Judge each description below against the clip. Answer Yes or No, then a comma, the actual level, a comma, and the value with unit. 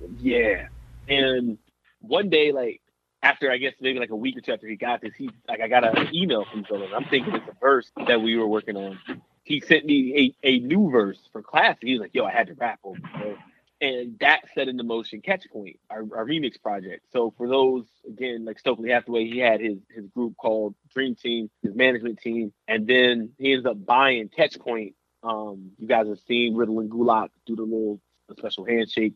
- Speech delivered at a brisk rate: Yes, fast, 220 wpm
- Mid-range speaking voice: No, low, 120 Hz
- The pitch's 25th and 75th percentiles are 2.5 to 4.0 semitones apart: Yes, average, 2.9 semitones